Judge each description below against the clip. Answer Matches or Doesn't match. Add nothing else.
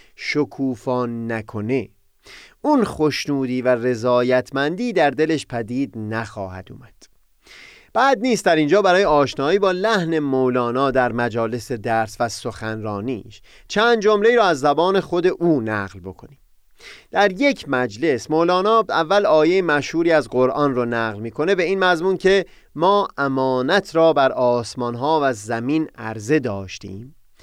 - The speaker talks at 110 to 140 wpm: Matches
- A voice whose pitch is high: Doesn't match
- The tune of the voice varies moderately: Doesn't match